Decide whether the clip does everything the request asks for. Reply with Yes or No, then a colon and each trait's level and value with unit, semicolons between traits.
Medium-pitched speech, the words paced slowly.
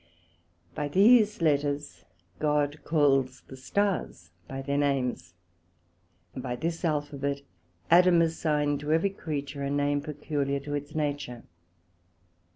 Yes: medium, 145 Hz; slow, 120 wpm